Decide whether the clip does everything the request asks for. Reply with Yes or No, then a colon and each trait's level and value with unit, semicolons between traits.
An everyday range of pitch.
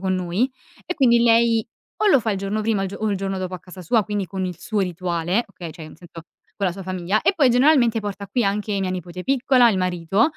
Yes: average, 3.9 semitones